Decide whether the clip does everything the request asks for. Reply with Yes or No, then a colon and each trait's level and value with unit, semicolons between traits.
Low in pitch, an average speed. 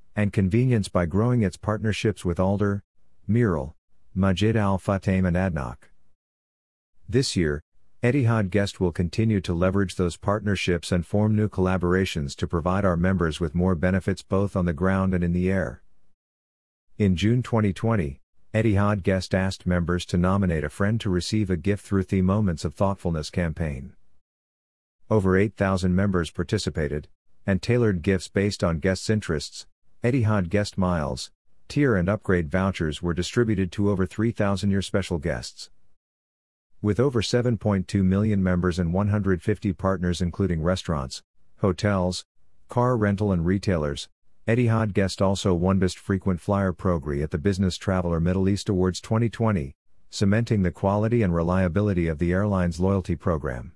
Yes: very low, 95 Hz; average, 145 wpm